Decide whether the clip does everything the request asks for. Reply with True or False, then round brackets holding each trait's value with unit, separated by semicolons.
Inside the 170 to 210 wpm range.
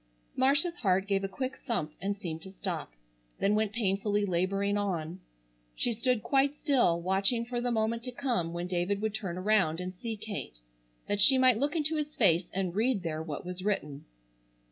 True (190 wpm)